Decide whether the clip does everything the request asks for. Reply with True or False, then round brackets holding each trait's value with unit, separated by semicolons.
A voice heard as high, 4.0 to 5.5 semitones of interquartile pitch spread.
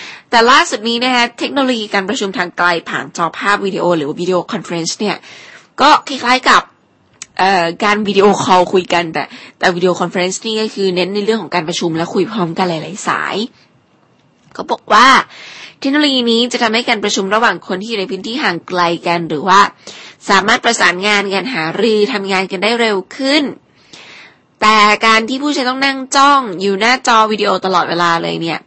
True (205 Hz; 4.5 semitones)